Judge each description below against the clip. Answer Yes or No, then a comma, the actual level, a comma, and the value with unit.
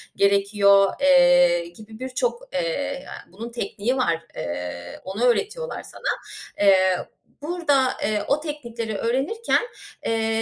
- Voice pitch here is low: No, high, 230 Hz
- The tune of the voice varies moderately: No, wide, 5.9 semitones